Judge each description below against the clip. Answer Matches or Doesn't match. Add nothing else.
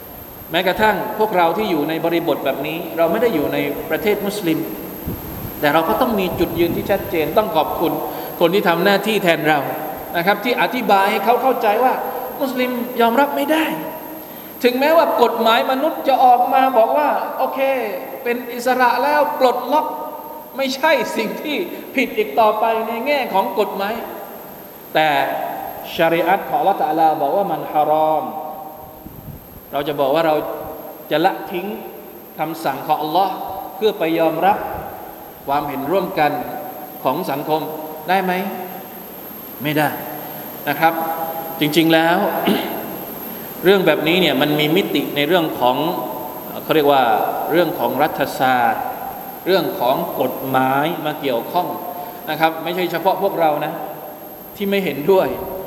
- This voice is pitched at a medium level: Matches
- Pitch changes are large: Matches